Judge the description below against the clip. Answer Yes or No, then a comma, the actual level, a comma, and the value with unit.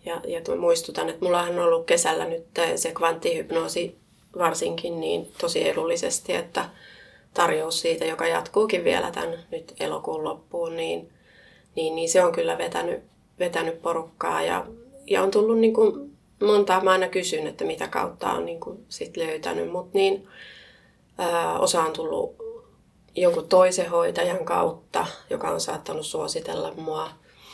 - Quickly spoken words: No, average, 145 wpm